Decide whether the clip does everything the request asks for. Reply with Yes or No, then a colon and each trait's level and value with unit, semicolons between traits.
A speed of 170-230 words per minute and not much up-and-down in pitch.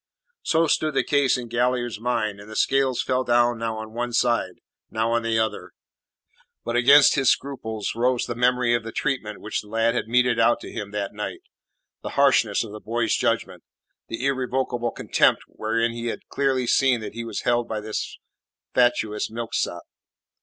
Yes: average, 180 wpm; narrow, 2.0 semitones